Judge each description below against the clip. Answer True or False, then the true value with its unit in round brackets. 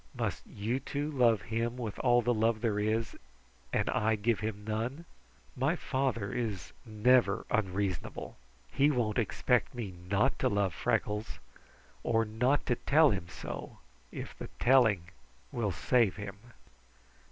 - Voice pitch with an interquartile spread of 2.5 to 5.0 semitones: True (3.2 semitones)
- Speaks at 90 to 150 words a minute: True (140 wpm)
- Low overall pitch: True (115 Hz)